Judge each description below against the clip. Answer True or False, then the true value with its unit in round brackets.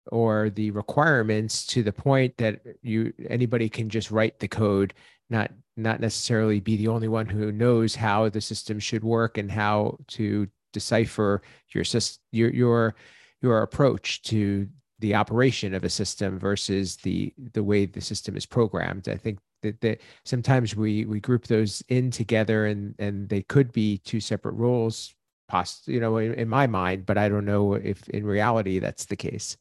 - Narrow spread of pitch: True (1.9 semitones)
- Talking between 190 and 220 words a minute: False (170 wpm)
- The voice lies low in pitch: True (110 Hz)